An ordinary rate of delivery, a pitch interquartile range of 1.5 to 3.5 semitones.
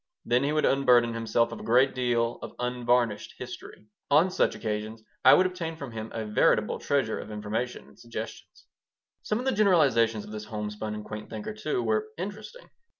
No: average, 185 wpm; average, 4.5 semitones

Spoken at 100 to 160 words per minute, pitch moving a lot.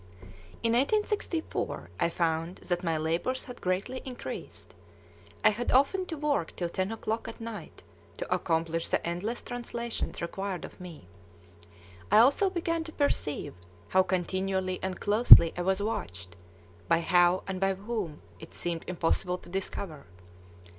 Yes: average, 145 wpm; wide, 5.7 semitones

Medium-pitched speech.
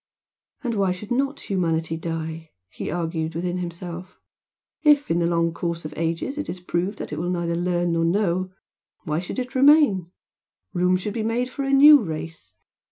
Yes: medium, 175 Hz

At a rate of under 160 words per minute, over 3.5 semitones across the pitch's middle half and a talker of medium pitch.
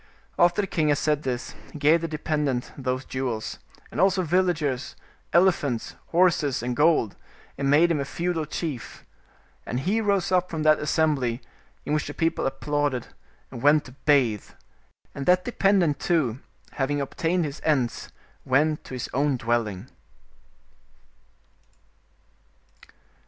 Yes: average, 140 wpm; average, 4.3 semitones; medium, 150 Hz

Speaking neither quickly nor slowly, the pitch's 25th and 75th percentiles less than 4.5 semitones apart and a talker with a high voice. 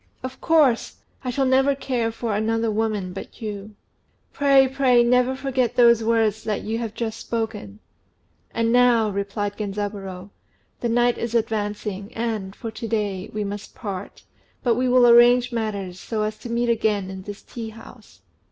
Yes: average, 165 wpm; average, 2.7 semitones; high, 225 Hz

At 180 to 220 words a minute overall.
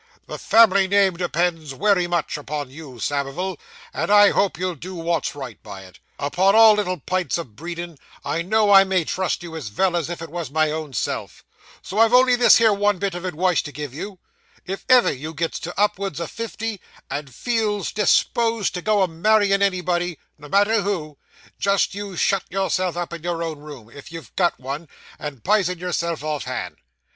Yes: average, 195 wpm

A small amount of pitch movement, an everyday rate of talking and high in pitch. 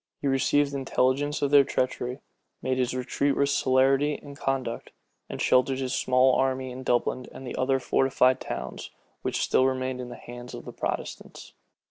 No: narrow, 1.2 semitones; average, 170 wpm; low, 130 Hz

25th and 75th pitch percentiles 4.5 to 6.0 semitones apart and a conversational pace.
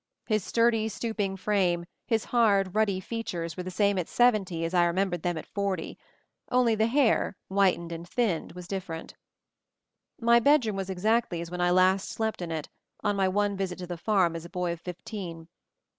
No: average, 3.7 semitones; average, 190 wpm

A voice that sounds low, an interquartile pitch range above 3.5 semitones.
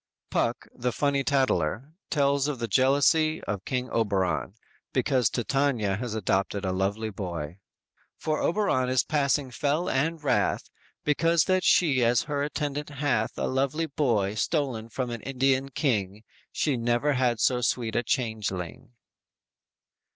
Yes: low, 130 Hz; average, 4.5 semitones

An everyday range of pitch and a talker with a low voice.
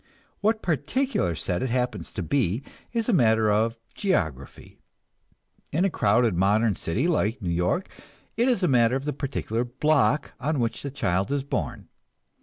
No: wide, 6.5 semitones; low, 125 Hz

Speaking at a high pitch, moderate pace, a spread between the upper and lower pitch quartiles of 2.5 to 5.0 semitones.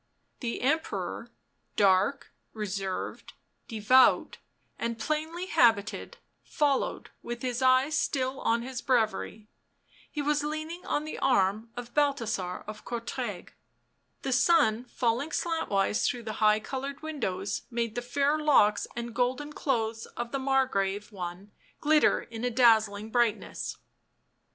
No: high, 240 Hz; slow, 125 wpm; average, 4.6 semitones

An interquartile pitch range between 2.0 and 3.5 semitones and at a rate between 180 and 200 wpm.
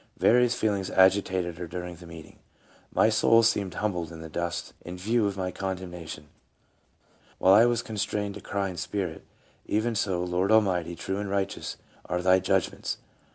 Yes: average, 2.8 semitones; average, 185 wpm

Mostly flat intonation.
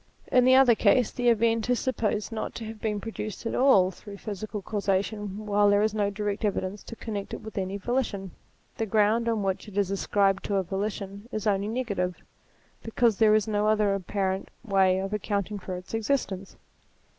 Yes: narrow, 2.2 semitones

